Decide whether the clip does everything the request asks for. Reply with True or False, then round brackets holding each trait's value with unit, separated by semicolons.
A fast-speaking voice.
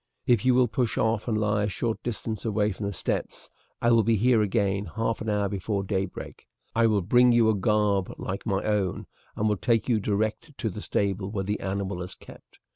True (215 wpm)